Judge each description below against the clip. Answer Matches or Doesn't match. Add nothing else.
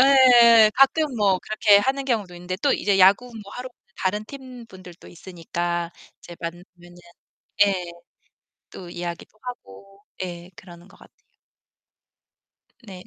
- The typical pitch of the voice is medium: Doesn't match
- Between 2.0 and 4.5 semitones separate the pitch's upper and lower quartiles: Doesn't match